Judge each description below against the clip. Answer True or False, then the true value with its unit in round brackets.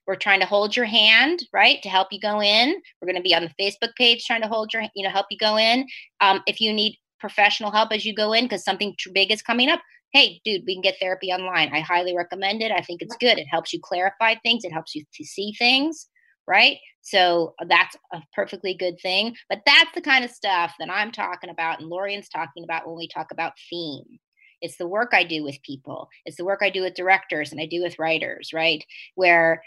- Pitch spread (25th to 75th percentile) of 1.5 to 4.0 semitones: False (4.4 semitones)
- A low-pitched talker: False (195 Hz)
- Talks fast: True (245 wpm)